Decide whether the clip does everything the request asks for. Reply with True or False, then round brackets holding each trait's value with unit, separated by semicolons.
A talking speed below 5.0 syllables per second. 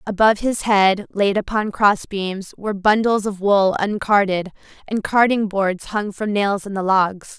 True (4.7 syllables/s)